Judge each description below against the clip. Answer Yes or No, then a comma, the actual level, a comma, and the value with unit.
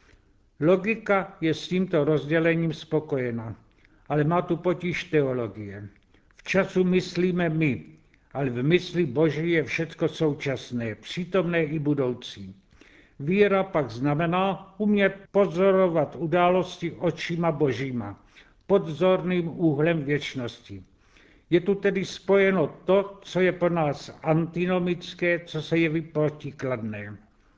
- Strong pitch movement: Yes, wide, 6.0 semitones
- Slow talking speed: Yes, slow, 110 wpm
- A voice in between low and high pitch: Yes, medium, 160 Hz